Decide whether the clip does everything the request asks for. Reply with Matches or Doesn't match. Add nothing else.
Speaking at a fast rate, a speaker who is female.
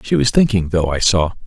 Doesn't match